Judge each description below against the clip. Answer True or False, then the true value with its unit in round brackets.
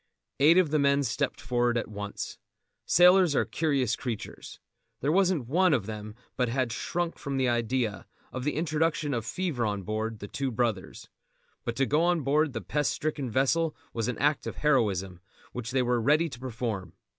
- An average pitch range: True (4.9 semitones)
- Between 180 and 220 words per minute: True (185 wpm)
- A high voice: False (130 Hz)